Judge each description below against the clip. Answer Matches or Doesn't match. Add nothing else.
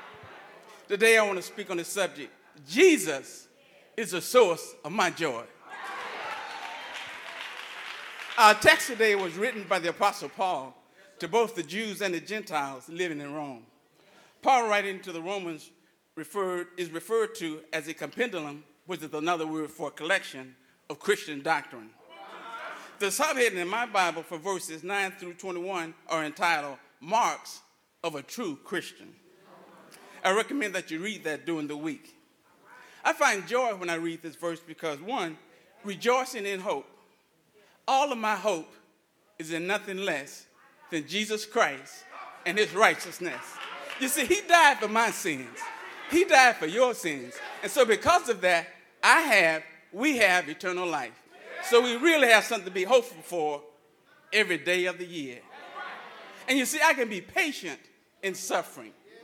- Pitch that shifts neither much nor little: Doesn't match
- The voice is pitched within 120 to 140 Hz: Doesn't match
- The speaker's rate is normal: Matches